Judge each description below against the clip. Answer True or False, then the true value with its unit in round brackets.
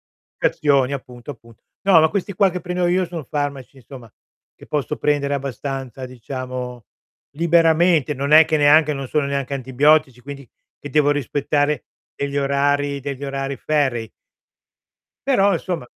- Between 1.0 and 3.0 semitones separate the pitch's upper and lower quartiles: True (2.4 semitones)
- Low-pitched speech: False (145 Hz)